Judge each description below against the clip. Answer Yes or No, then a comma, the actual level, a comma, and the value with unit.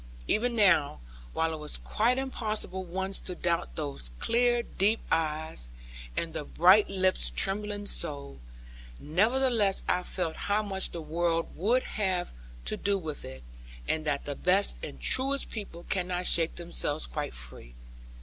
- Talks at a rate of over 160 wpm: No, average, 150 wpm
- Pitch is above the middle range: No, medium, 180 Hz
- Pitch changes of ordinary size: Yes, average, 4.9 semitones